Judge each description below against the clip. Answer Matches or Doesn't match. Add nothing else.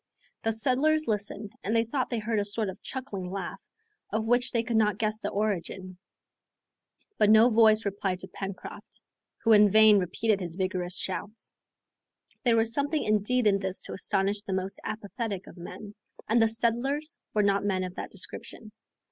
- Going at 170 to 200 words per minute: Matches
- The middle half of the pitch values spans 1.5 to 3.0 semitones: Matches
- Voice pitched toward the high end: Matches